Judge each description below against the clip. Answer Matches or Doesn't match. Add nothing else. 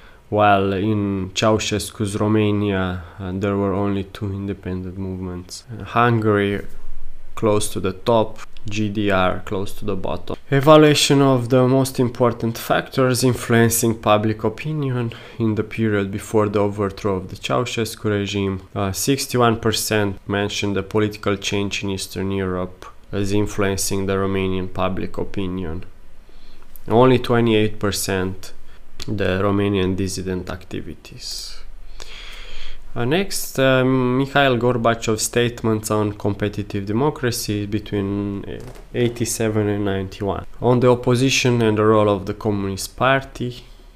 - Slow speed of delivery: Matches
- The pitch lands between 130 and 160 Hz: Doesn't match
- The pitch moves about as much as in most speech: Matches